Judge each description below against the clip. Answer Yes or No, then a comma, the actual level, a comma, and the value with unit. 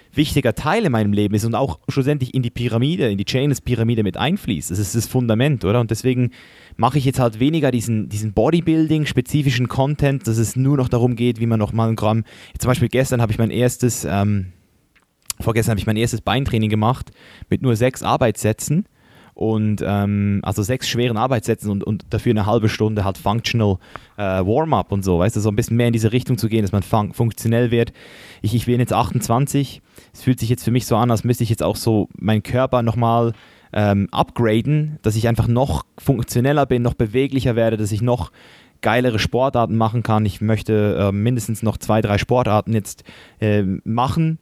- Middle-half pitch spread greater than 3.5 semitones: No, average, 2.8 semitones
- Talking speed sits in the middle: No, fast, 200 wpm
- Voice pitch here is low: Yes, low, 115 Hz